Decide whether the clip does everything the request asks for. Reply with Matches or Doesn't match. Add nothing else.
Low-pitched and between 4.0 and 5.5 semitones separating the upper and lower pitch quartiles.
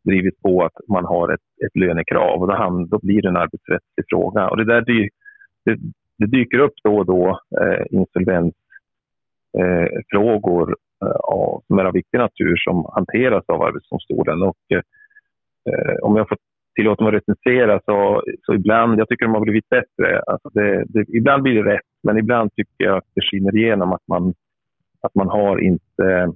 Matches